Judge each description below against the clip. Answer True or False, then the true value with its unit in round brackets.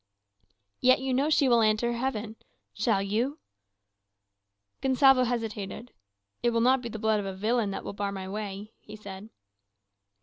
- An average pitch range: True (3.4 semitones)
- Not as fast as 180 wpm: True (160 wpm)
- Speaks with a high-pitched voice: True (225 Hz)